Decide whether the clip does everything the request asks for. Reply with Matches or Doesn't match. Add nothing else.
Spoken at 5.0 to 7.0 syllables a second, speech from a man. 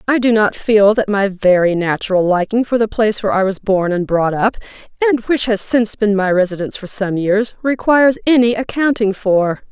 Doesn't match